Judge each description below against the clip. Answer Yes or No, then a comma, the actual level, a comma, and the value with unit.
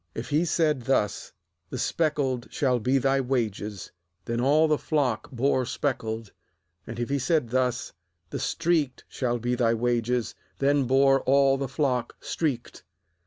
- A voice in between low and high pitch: No, low, 130 Hz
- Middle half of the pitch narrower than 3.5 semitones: Yes, average, 2.8 semitones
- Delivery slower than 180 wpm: Yes, average, 150 wpm